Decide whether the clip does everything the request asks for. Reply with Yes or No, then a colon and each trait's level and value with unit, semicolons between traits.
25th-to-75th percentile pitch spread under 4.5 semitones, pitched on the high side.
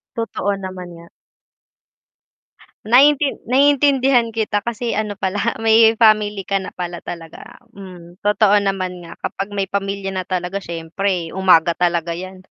Yes: average, 3.5 semitones; high, 195 Hz